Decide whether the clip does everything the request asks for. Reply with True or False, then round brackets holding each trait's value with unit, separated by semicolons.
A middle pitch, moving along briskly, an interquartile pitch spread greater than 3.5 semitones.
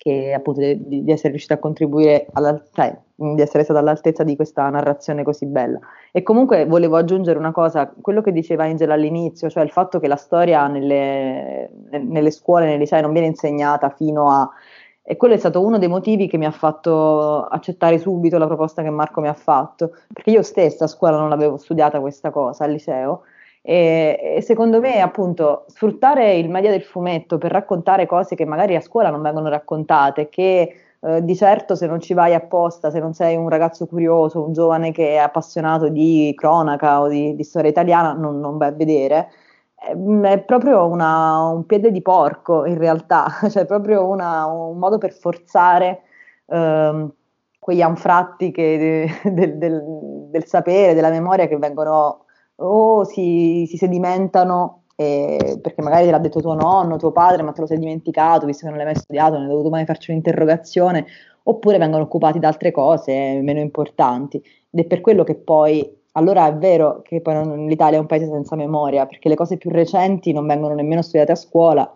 False (160 Hz; 190 wpm; 2.6 semitones)